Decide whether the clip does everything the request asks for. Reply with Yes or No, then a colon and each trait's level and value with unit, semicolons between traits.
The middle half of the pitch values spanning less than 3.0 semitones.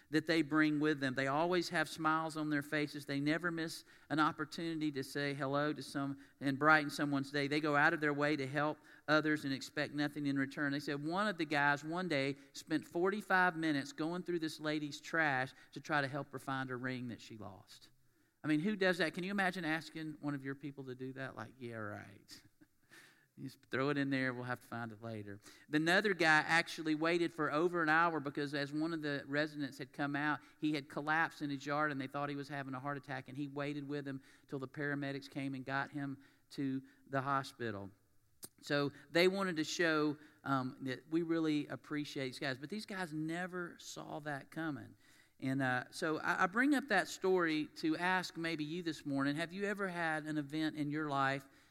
Yes: narrow, 2.5 semitones